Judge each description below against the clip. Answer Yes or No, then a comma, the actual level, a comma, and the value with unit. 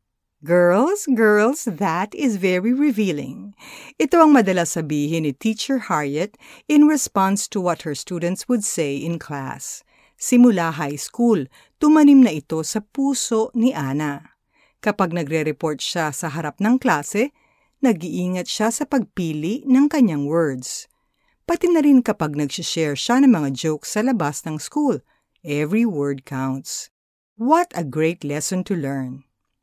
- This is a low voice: No, medium, 185 Hz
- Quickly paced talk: No, average, 140 wpm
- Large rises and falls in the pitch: Yes, wide, 8.1 semitones